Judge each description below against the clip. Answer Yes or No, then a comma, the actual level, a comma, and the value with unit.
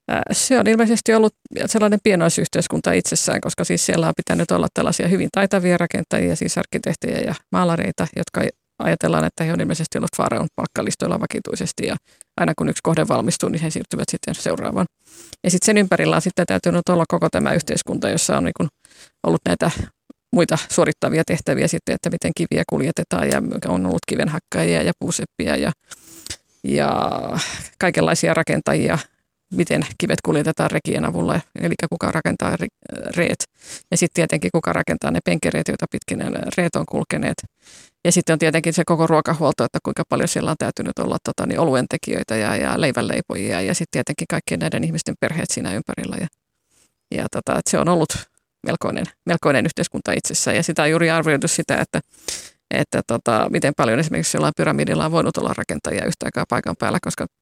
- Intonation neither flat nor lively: Yes, average, 3.3 semitones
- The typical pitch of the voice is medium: Yes, medium, 170 Hz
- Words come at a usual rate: No, fast, 165 wpm